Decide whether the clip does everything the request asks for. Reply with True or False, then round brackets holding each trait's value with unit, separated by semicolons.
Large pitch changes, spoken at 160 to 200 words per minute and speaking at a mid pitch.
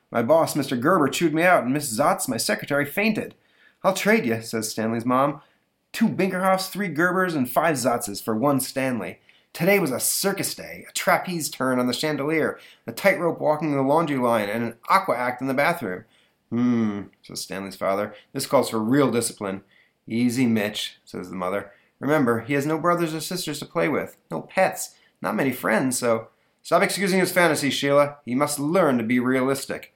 True (6.7 semitones; 190 wpm; 145 Hz)